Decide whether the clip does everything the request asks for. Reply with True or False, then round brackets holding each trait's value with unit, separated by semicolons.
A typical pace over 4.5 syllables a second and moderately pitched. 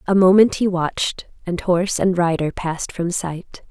True (4.8 syllables/s; 180 Hz)